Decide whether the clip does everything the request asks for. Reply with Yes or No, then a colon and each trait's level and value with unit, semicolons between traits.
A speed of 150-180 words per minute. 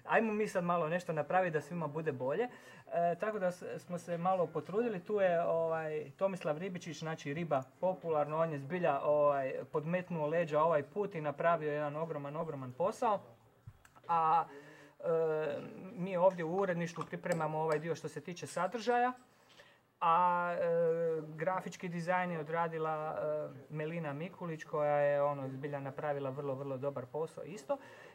Yes: average, 155 wpm